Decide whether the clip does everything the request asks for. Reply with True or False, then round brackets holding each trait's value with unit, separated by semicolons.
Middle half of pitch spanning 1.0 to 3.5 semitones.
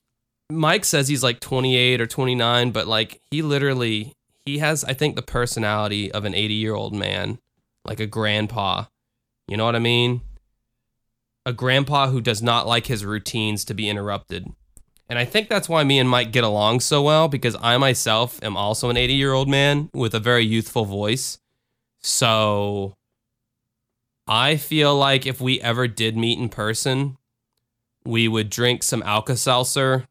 True (2.9 semitones)